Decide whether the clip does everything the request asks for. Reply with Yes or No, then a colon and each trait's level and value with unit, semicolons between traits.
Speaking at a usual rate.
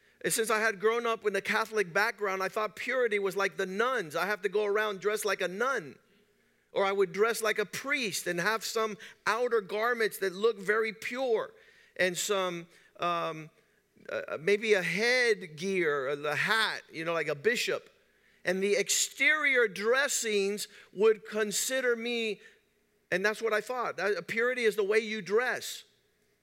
Yes: average, 170 wpm